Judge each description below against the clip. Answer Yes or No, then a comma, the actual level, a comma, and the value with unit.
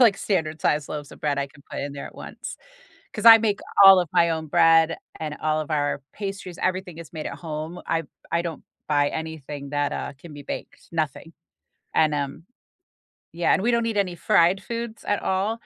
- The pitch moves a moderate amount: Yes, average, 4.1 semitones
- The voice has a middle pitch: Yes, medium, 165 Hz